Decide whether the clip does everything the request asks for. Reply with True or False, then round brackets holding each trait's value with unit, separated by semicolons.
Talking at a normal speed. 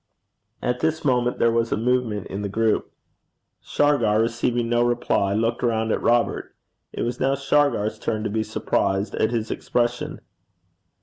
True (160 wpm)